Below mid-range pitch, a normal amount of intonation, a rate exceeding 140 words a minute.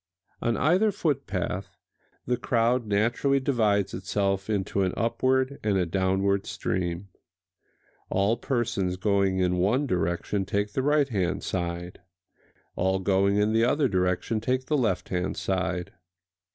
No: low, 100 Hz; average, 4.3 semitones; slow, 135 wpm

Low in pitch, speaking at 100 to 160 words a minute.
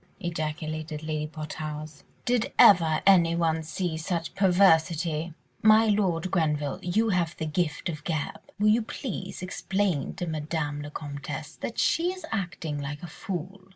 No: medium, 165 Hz; average, 150 wpm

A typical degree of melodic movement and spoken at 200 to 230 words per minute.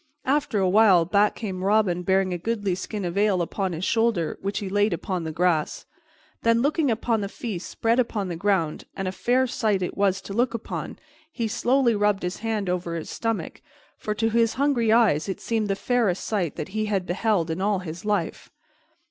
Yes: average, 3.8 semitones; fast, 205 wpm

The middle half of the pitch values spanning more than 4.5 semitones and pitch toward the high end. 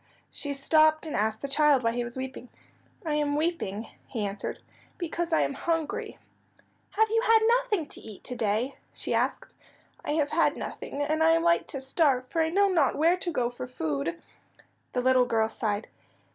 Yes: average, 5.2 semitones; very high, 285 Hz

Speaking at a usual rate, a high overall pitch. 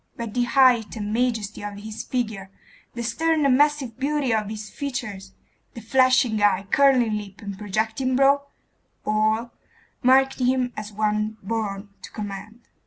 Yes: average, 150 wpm; high, 225 Hz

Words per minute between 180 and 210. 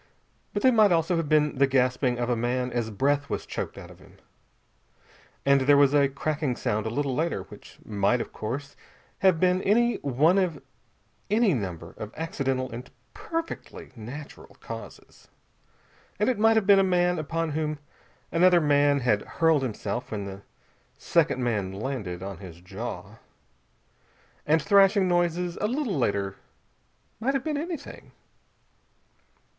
No: average, 155 wpm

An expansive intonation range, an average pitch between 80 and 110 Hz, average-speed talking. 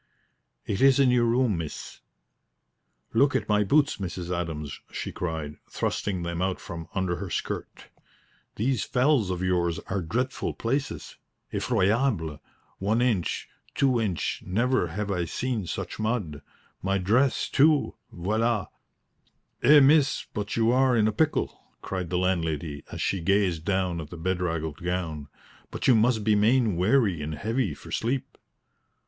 Yes: wide, 5.8 semitones; low, 100 Hz; average, 150 wpm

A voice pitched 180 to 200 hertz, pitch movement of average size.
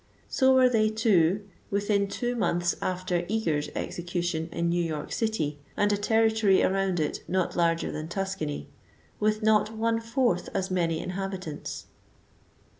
Yes: high, 190 Hz; average, 4.2 semitones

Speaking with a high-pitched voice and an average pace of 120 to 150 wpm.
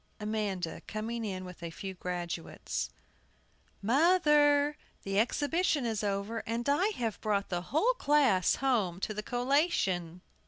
Yes: high, 220 Hz; slow, 135 wpm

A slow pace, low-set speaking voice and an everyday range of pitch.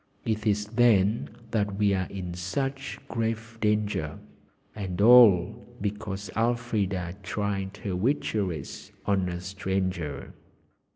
Yes: slow, 110 wpm; low, 100 Hz; average, 3.1 semitones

